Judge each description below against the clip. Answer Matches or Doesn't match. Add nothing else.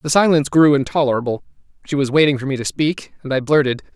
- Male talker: Matches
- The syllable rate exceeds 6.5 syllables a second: Matches